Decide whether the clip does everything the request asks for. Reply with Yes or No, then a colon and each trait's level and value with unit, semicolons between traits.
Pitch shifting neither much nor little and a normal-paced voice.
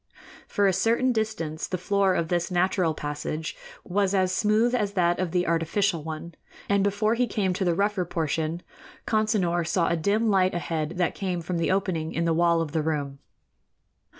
Yes: average, 3.4 semitones; average, 185 wpm